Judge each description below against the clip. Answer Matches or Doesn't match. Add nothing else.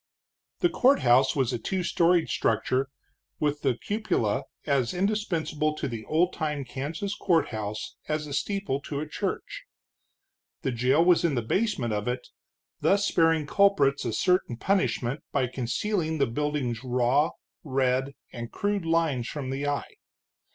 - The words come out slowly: Doesn't match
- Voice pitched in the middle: Matches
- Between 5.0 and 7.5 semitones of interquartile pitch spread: Matches